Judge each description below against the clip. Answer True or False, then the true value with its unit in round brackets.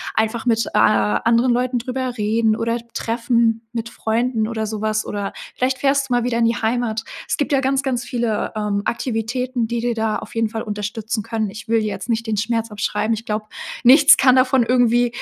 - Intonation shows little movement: True (2.1 semitones)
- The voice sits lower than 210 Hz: False (230 Hz)